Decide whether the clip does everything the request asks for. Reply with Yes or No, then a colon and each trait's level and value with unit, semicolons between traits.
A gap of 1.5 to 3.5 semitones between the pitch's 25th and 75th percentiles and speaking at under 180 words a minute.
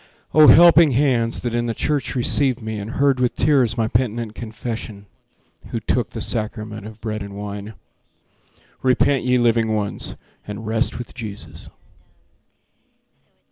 Yes: average, 2.8 semitones; average, 140 wpm